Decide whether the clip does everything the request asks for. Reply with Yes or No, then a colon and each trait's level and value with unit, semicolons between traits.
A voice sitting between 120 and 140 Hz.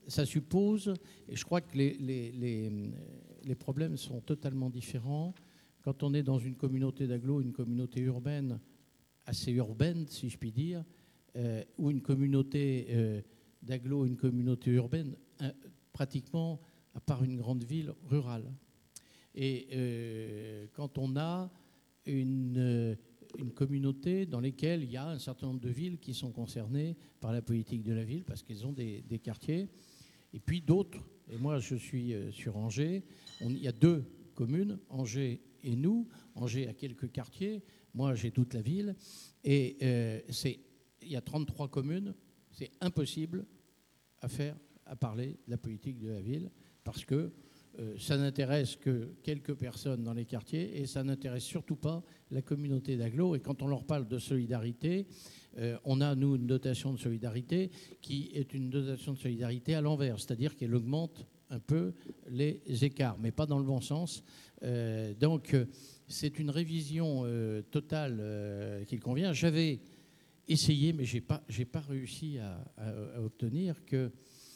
Yes: low, 135 Hz